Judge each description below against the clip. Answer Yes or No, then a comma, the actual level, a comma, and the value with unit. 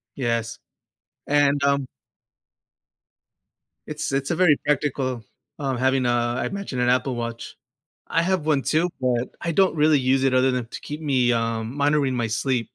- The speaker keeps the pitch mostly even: No, average, 3.3 semitones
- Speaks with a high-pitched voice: No, low, 135 Hz